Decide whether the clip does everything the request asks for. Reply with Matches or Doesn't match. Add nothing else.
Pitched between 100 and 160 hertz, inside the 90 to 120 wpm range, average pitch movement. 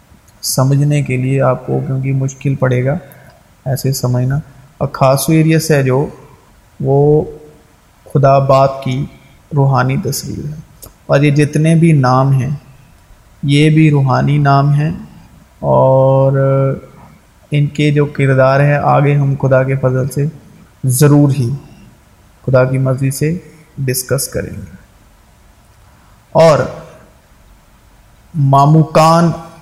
Doesn't match